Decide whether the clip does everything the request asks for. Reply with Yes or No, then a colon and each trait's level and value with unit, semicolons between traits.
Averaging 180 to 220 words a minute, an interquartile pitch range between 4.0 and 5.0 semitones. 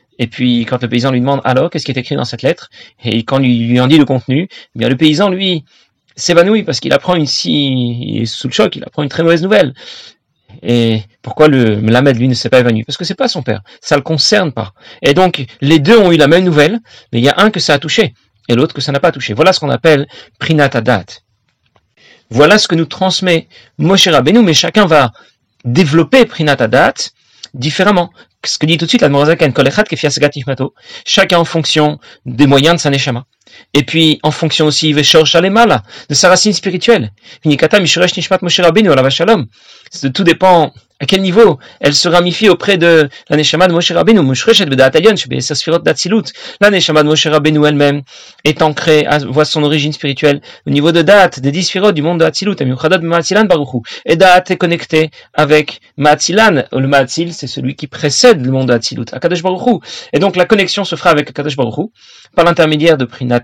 Yes: average, 200 wpm; average, 4.7 semitones